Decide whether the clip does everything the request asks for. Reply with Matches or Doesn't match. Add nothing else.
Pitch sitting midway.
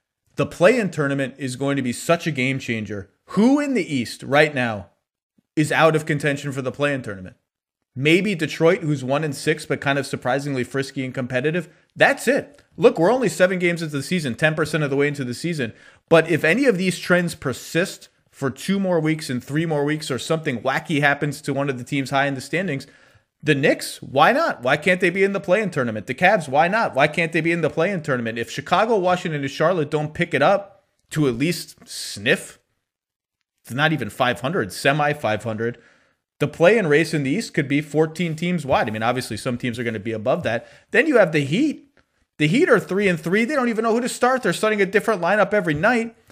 Matches